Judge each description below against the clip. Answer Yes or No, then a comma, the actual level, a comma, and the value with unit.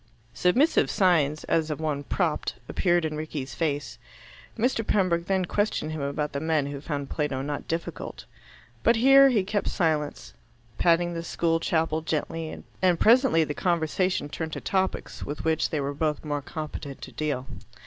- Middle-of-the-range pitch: Yes, medium, 160 Hz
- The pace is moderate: Yes, average, 165 wpm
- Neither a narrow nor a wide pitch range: Yes, average, 3.4 semitones